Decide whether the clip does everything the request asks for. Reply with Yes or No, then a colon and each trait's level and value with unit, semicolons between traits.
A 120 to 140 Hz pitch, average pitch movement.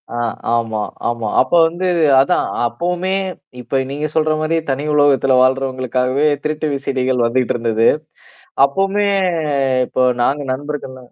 Yes: low, 135 Hz; average, 3.2 semitones